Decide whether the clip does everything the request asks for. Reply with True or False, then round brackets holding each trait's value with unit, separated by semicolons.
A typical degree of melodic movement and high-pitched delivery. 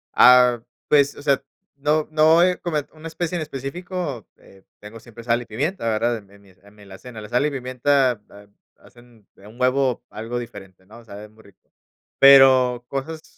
False (4.7 semitones; 125 Hz)